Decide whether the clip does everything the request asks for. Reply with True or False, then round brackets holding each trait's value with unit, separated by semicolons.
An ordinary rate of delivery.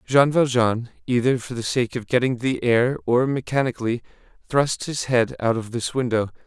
True (175 wpm)